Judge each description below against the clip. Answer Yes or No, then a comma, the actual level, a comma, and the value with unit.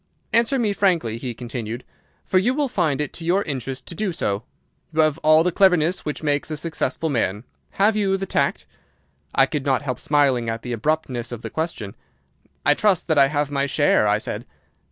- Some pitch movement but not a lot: No, wide, 5.8 semitones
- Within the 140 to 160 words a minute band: No, average, 200 wpm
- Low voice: No, medium, 150 Hz